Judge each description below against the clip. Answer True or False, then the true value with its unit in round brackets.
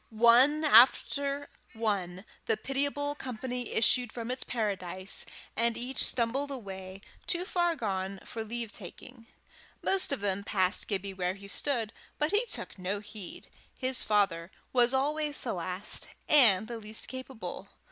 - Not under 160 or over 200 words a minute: False (145 wpm)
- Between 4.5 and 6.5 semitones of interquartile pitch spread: True (5.1 semitones)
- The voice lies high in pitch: True (230 Hz)